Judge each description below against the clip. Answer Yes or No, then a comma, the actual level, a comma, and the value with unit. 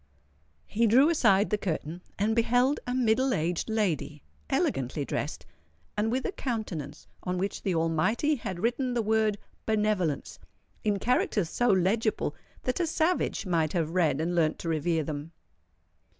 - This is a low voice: No, high, 200 Hz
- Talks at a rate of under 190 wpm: Yes, average, 150 wpm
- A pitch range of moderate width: No, wide, 6.1 semitones